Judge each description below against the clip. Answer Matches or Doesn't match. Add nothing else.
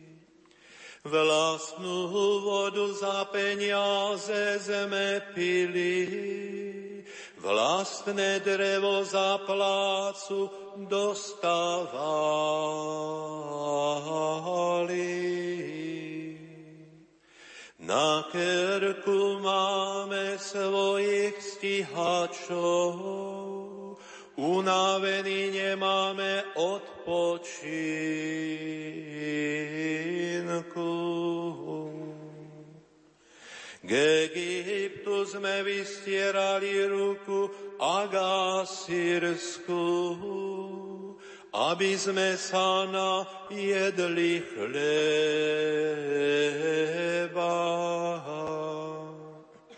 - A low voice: Doesn't match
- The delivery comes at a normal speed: Doesn't match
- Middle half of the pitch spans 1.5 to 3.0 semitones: Doesn't match